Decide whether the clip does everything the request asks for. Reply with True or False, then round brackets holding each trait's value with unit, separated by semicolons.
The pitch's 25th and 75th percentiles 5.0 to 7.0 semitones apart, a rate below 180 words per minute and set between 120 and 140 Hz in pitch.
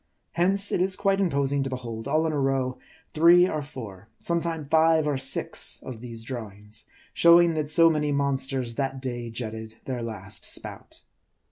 True (5.3 semitones; 165 wpm; 135 Hz)